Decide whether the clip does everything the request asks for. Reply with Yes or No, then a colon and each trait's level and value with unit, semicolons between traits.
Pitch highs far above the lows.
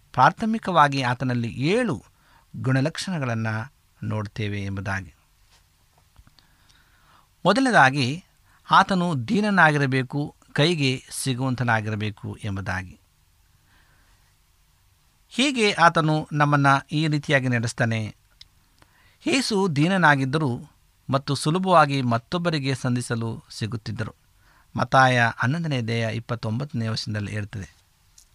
Yes: wide, 5.9 semitones